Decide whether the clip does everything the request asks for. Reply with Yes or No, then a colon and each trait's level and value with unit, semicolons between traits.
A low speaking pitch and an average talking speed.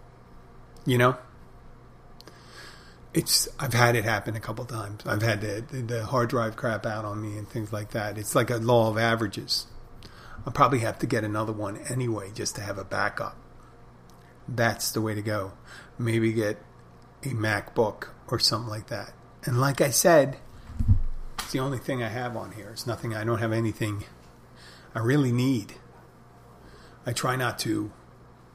Yes: low, 115 Hz; average, 170 wpm